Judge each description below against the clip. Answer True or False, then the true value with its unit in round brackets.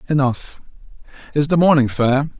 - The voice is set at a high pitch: False (140 Hz)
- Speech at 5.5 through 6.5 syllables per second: False (5.0 syllables/s)